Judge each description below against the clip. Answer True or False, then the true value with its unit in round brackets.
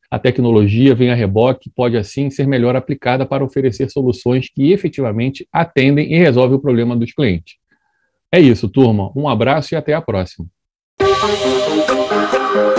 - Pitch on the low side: True (130 Hz)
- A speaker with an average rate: True (145 wpm)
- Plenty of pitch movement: False (3.4 semitones)